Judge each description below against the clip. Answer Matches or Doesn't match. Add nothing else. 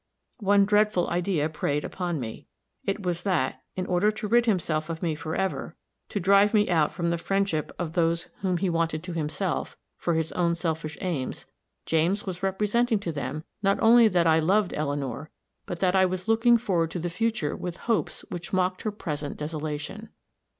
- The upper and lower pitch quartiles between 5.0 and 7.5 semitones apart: Doesn't match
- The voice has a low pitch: Doesn't match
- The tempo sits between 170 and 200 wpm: Matches